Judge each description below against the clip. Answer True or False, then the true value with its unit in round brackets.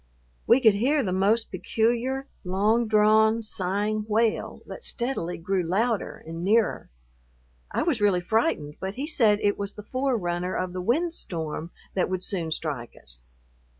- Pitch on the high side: True (210 Hz)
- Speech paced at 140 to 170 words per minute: True (150 wpm)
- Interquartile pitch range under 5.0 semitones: True (4.2 semitones)